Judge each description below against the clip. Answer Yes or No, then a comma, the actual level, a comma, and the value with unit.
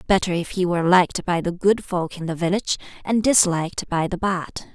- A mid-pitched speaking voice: Yes, medium, 180 Hz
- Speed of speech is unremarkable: No, fast, 215 wpm